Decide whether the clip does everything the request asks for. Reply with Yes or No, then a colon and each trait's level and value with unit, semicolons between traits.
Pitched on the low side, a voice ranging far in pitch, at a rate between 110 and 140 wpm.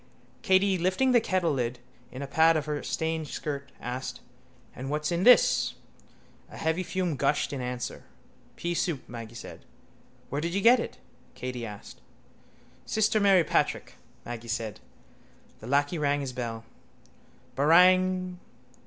No: medium, 150 Hz; wide, 6.3 semitones; slow, 135 wpm